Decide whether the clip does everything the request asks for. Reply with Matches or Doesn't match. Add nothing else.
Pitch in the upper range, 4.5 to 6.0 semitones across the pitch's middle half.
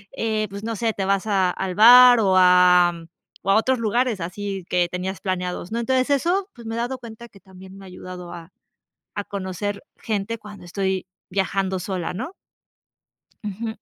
Doesn't match